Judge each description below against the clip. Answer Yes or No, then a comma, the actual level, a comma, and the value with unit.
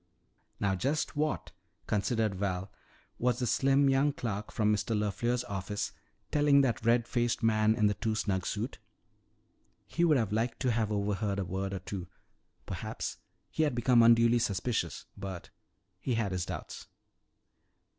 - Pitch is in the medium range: No, low, 110 Hz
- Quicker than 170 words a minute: No, average, 155 wpm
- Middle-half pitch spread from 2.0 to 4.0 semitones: Yes, average, 3.6 semitones